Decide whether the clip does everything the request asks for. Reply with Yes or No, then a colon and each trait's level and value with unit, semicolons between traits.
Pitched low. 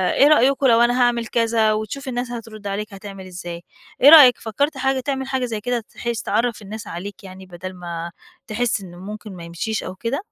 No: high, 220 Hz